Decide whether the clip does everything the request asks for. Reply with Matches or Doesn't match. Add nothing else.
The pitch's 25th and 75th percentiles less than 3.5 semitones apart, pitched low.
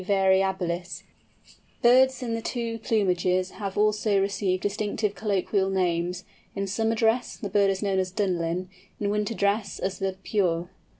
Doesn't match